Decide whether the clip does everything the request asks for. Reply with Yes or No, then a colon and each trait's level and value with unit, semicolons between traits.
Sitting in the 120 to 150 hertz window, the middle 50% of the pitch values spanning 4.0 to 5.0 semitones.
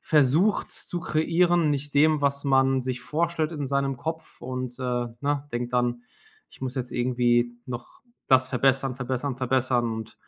No: low, 135 Hz; average, 2.9 semitones